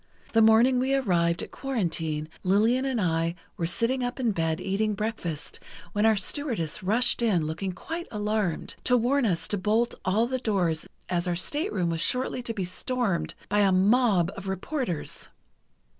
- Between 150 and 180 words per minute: Yes, average, 170 wpm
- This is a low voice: No, high, 210 Hz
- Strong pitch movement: Yes, wide, 5.7 semitones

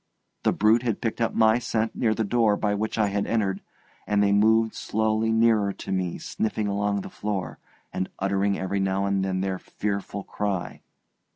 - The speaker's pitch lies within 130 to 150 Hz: No, low, 105 Hz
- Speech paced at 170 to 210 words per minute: Yes, average, 185 wpm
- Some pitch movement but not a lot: No, narrow, 2.0 semitones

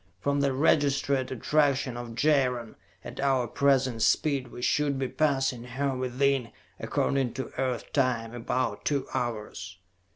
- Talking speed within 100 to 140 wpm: Yes, slow, 135 wpm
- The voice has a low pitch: Yes, low, 130 Hz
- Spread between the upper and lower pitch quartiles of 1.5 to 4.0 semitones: Yes, narrow, 2.4 semitones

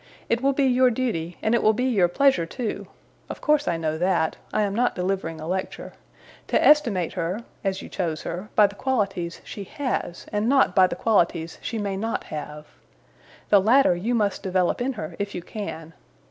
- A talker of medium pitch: No, high, 200 Hz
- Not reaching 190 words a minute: No, average, 200 wpm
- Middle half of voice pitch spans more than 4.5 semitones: Yes, wide, 5.4 semitones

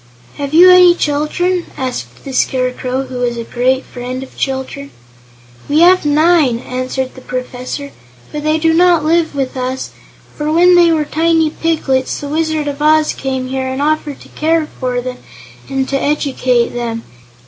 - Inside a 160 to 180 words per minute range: Yes, average, 170 wpm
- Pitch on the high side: Yes, very high, 280 Hz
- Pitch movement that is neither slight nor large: Yes, average, 3.6 semitones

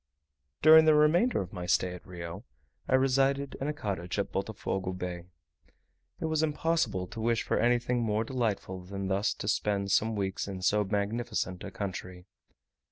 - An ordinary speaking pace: Yes, average, 165 wpm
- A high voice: No, low, 105 Hz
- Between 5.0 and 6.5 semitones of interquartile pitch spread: Yes, wide, 5.6 semitones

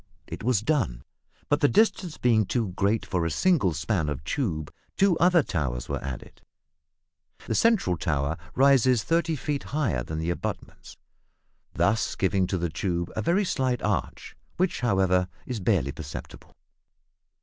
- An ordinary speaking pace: Yes, average, 150 wpm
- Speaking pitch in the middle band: No, low, 105 Hz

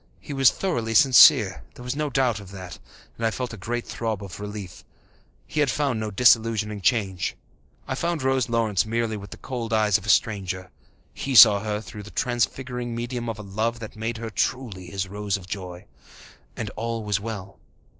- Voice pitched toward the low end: Yes, low, 110 Hz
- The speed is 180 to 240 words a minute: Yes, average, 195 wpm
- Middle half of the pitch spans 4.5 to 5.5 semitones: No, average, 3.1 semitones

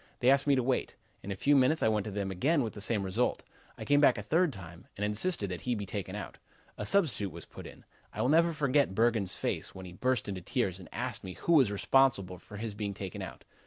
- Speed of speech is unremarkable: No, fast, 255 wpm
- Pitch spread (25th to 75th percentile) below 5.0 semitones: No, wide, 5.6 semitones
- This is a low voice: Yes, low, 110 Hz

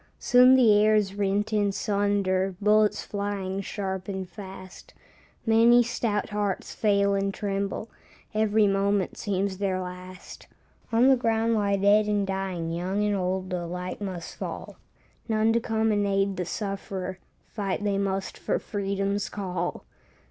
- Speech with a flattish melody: Yes, narrow, 1.7 semitones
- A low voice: No, high, 200 Hz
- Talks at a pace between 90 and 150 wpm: Yes, average, 145 wpm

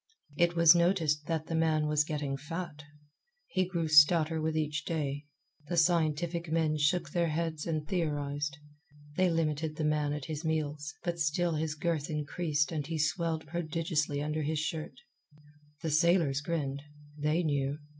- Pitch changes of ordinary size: No, narrow, 1.9 semitones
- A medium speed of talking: Yes, average, 155 wpm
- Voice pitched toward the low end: No, medium, 155 Hz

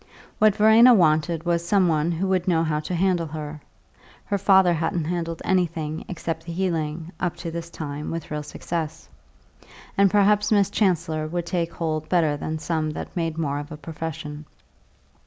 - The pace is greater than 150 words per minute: Yes, average, 175 wpm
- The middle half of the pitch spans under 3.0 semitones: Yes, narrow, 2.6 semitones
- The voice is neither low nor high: Yes, medium, 165 Hz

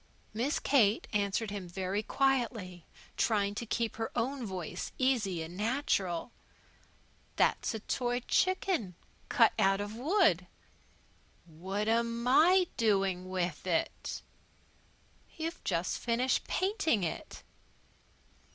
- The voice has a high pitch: Yes, high, 220 Hz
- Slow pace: Yes, slow, 105 wpm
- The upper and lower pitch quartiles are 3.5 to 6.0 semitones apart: Yes, average, 5.2 semitones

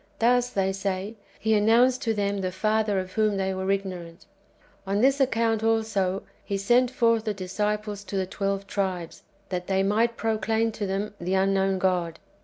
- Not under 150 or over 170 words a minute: No, average, 180 wpm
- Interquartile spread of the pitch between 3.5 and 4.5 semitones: No, average, 2.7 semitones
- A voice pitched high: Yes, high, 200 Hz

